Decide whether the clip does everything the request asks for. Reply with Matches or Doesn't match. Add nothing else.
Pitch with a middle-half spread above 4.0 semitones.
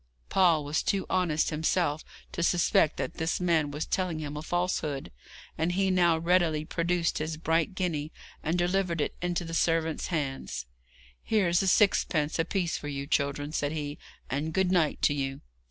Doesn't match